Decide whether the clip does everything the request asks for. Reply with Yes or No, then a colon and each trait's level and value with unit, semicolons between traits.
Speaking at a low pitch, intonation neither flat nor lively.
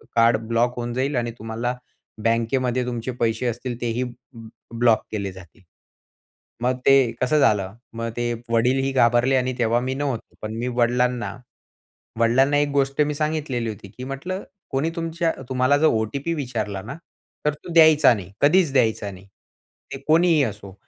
Yes: low, 125 Hz; average, 3.1 semitones